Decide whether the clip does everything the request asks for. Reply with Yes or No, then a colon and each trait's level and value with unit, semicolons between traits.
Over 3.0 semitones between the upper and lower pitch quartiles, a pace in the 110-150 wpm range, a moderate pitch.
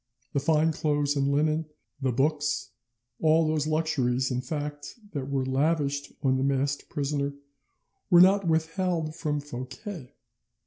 No: narrow, 2.4 semitones; slow, 135 wpm; medium, 145 Hz